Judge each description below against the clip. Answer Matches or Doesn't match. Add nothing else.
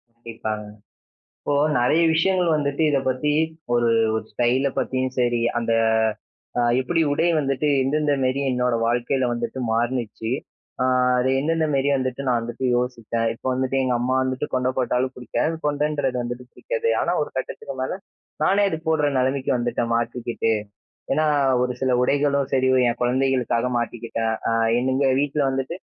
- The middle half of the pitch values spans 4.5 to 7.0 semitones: Doesn't match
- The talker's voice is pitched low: Matches